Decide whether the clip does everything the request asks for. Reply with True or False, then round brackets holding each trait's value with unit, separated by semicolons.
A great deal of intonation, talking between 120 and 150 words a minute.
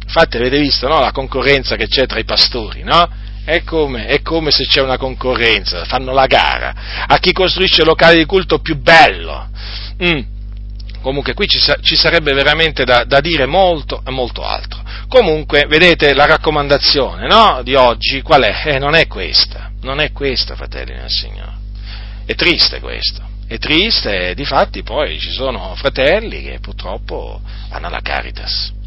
False (7.0 semitones; 170 wpm)